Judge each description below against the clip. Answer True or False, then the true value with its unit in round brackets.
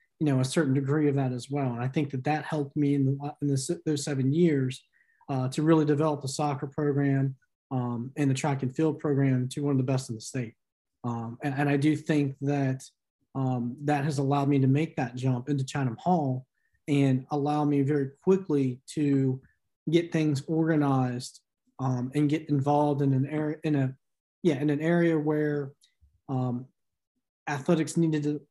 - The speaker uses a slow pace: False (190 wpm)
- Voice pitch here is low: False (145 Hz)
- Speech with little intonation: True (2.3 semitones)